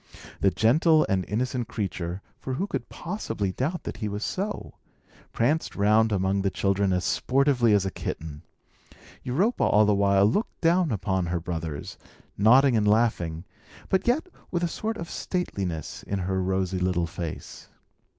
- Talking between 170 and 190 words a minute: No, average, 160 wpm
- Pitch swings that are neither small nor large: No, wide, 6.6 semitones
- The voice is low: Yes, low, 105 Hz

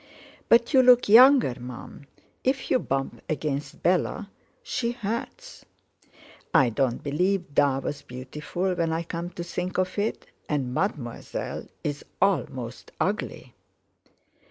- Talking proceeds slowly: Yes, slow, 120 wpm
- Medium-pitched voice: Yes, medium, 170 Hz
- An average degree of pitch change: No, wide, 6.9 semitones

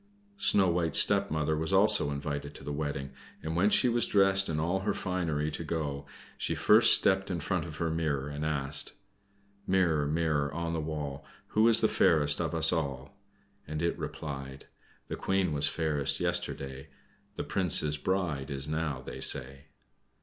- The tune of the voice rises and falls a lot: No, average, 4.0 semitones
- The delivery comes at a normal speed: Yes, average, 170 wpm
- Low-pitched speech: Yes, very low, 80 Hz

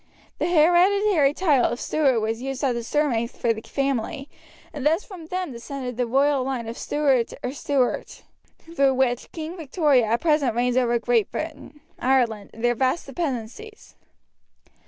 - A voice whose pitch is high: Yes, very high, 270 Hz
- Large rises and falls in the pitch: No, average, 4.3 semitones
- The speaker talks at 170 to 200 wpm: No, average, 160 wpm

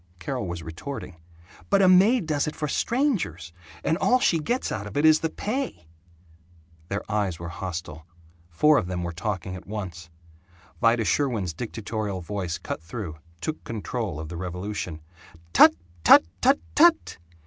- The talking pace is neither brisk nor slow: Yes, average, 160 wpm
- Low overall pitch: Yes, low, 100 Hz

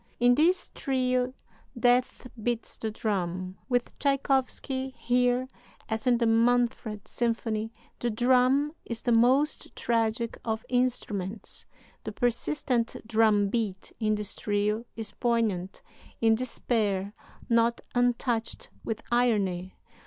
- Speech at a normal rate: No, slow, 115 wpm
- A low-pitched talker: No, high, 235 Hz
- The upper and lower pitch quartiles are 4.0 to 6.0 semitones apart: No, narrow, 2.4 semitones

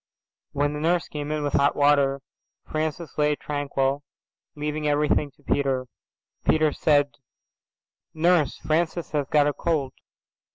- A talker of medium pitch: Yes, medium, 150 Hz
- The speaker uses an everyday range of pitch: No, narrow, 1.4 semitones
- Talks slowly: Yes, slow, 130 wpm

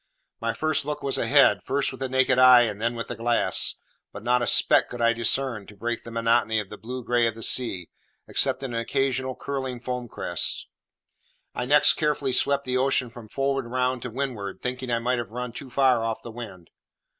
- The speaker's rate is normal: No, fast, 210 wpm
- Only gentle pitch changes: Yes, narrow, 2.2 semitones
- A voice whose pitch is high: No, low, 125 Hz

